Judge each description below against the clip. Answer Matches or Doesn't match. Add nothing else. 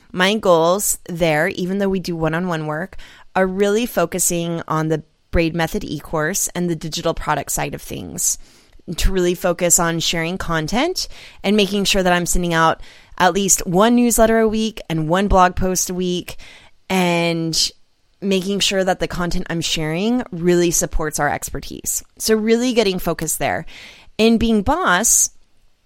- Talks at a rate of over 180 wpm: Doesn't match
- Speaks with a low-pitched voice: Doesn't match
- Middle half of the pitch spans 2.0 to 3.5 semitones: Matches